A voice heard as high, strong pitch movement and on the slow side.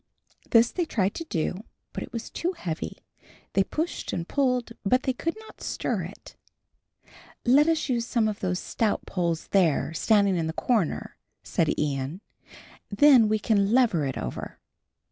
No: high, 215 Hz; wide, 6.1 semitones; average, 165 wpm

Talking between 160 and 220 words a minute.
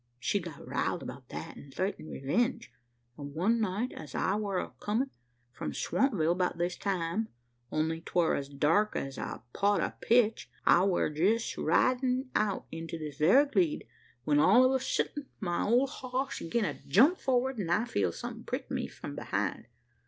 Yes: average, 175 wpm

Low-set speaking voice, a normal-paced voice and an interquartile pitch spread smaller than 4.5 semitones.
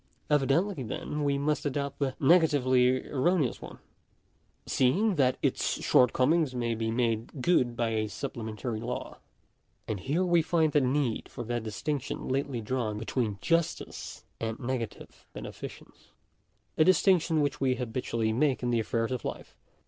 Yes: low, 130 Hz; average, 150 wpm; average, 4.1 semitones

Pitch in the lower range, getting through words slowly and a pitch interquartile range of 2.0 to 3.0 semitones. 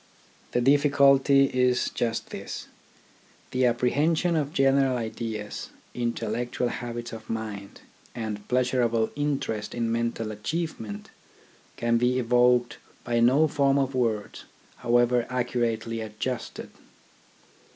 Yes: low, 120 Hz; slow, 105 wpm; average, 2.7 semitones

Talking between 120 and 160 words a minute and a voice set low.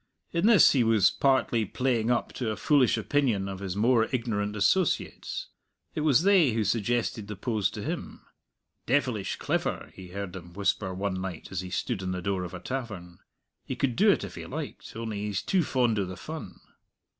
No: average, 195 wpm; low, 110 Hz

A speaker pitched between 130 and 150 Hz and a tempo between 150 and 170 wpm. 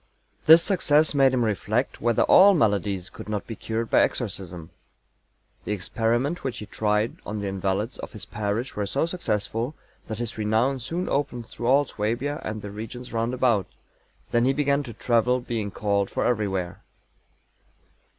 No: low, 115 Hz; average, 160 wpm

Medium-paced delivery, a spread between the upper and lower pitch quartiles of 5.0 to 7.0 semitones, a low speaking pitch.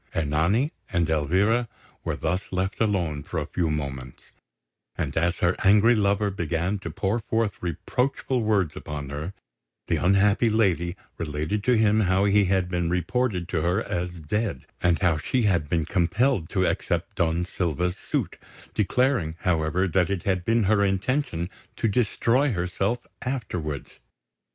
No: average, 150 wpm; average, 4.1 semitones; very low, 95 Hz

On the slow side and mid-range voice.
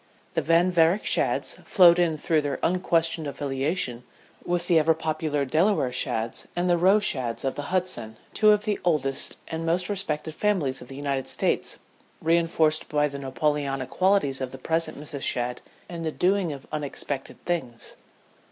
No: average, 165 wpm; medium, 155 Hz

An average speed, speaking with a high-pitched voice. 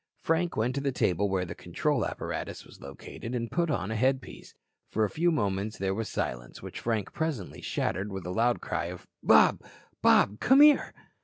No: average, 190 wpm; low, 110 Hz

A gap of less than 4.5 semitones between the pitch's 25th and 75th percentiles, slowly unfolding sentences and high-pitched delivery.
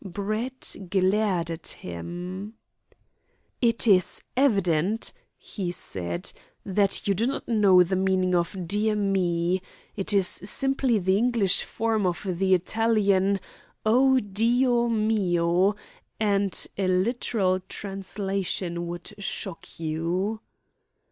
Yes: average, 3.1 semitones; slow, 110 wpm; high, 195 Hz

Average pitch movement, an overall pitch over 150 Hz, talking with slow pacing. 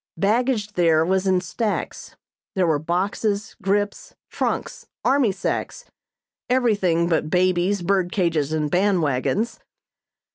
Yes: average, 3.4 semitones; high, 190 Hz; slow, 115 wpm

